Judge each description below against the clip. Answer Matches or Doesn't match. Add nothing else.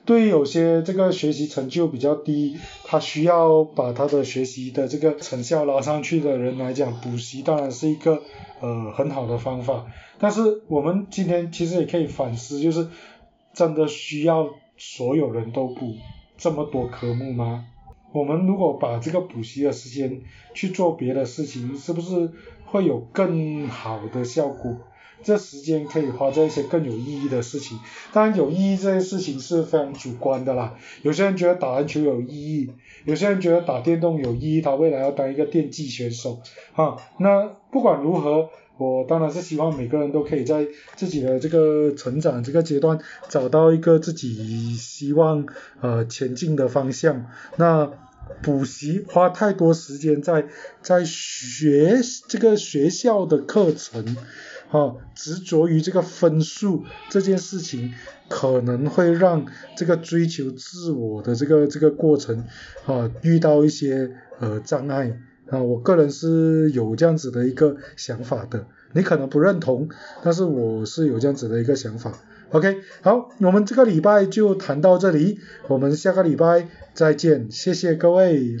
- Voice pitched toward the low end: Doesn't match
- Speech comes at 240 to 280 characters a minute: Matches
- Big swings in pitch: Doesn't match